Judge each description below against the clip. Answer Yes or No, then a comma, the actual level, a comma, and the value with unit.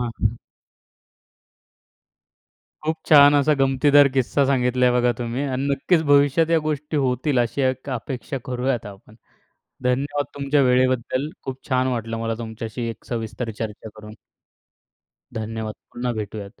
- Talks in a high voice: No, low, 130 Hz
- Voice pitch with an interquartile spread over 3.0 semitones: Yes, average, 3.4 semitones